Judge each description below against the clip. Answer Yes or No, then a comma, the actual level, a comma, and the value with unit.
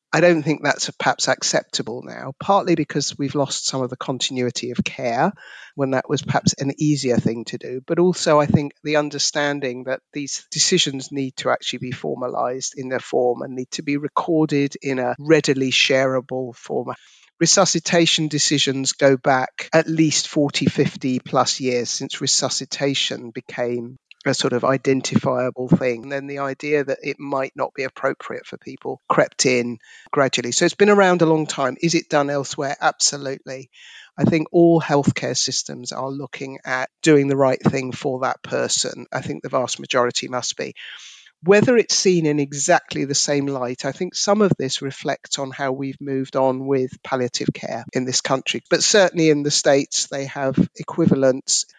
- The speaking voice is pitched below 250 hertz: Yes, medium, 140 Hz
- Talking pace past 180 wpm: No, average, 175 wpm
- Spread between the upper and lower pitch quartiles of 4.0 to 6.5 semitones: No, average, 2.8 semitones